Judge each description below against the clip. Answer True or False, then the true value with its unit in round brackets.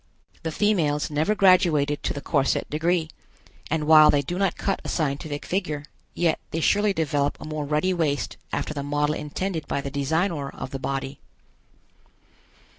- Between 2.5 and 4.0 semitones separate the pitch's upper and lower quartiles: True (3.2 semitones)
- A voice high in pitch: False (155 Hz)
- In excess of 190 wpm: False (165 wpm)